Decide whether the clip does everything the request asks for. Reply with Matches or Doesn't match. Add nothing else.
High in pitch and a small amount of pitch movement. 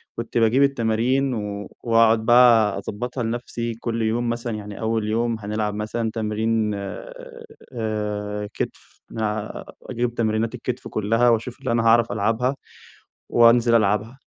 Doesn't match